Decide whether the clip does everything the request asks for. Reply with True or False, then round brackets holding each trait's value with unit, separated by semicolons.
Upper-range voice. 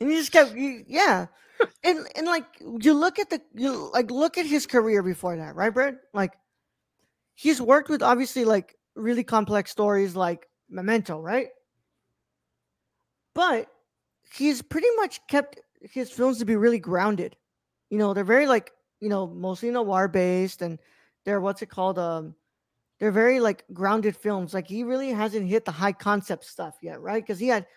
True (225 Hz)